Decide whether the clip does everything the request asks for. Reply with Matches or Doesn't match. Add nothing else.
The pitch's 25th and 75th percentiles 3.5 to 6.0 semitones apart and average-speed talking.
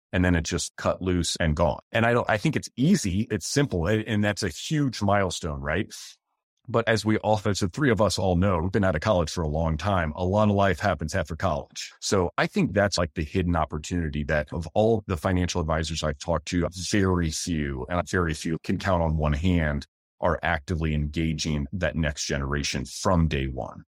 Doesn't match